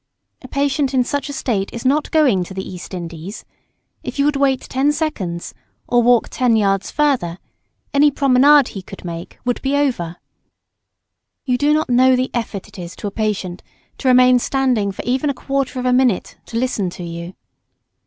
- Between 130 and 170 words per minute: No, average, 190 wpm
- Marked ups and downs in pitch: Yes, wide, 6.0 semitones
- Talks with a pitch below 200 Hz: No, very high, 250 Hz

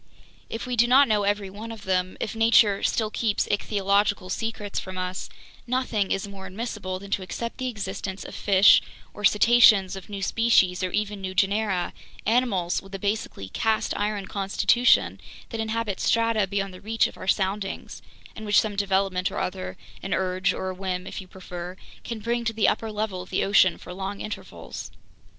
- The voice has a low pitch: No, high, 200 Hz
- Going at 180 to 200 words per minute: Yes, average, 185 wpm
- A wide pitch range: No, average, 2.7 semitones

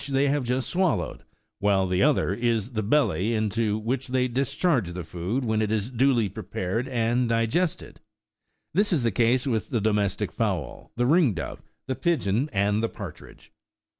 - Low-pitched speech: Yes, low, 115 Hz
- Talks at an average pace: Yes, average, 165 wpm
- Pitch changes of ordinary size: Yes, average, 4.2 semitones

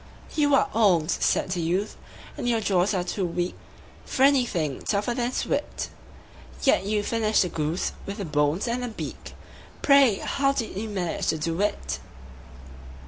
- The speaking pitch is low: No, high, 200 Hz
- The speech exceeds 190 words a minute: No, average, 165 wpm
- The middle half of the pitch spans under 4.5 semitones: No, wide, 5.5 semitones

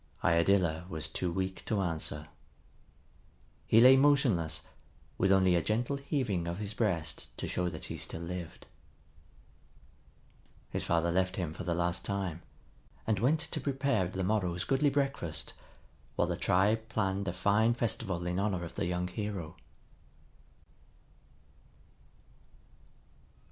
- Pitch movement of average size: Yes, average, 4.2 semitones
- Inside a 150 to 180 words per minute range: No, slow, 135 wpm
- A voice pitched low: Yes, very low, 95 Hz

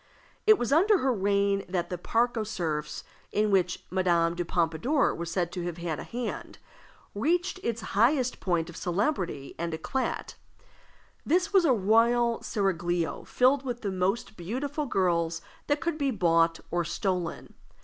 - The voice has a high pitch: Yes, high, 195 Hz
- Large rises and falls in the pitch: Yes, wide, 6.5 semitones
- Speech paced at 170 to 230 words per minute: No, average, 160 wpm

